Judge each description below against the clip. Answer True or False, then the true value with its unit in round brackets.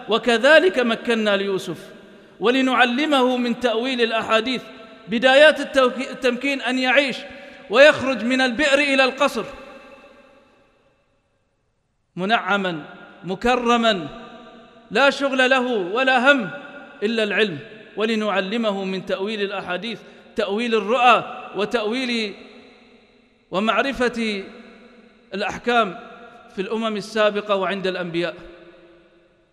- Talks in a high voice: True (230 Hz)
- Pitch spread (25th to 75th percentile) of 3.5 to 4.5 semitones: True (4.2 semitones)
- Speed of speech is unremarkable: False (80 wpm)